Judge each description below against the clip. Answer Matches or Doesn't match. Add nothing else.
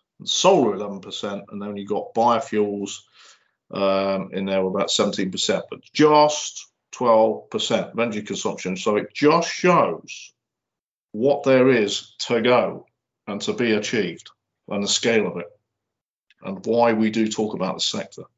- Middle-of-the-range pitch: Doesn't match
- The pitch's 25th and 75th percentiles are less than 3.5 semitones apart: Matches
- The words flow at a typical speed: Matches